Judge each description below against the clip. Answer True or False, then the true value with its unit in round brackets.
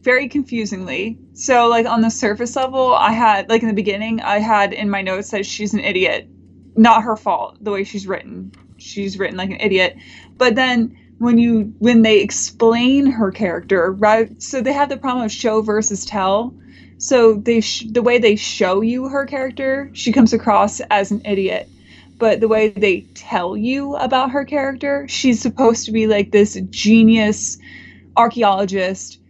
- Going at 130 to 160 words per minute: False (180 wpm)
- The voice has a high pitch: True (220 Hz)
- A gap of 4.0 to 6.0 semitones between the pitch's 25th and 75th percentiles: False (3.3 semitones)